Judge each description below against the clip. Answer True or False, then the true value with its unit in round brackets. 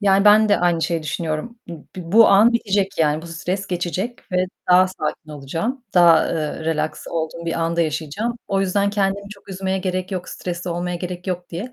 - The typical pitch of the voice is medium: True (180 Hz)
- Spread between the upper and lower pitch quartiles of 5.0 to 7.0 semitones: False (3.1 semitones)